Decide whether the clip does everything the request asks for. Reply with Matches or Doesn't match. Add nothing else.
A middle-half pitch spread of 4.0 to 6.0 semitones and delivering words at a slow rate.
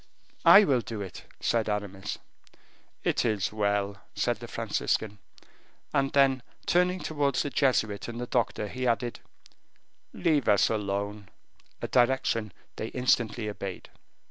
Matches